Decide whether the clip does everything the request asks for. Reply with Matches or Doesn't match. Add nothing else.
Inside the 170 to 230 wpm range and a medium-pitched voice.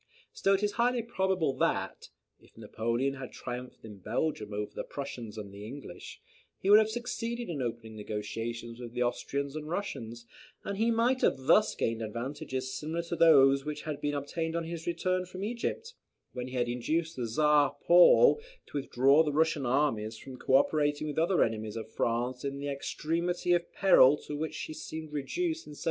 Matches